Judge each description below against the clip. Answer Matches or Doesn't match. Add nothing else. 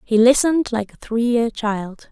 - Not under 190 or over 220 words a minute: Matches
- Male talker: Doesn't match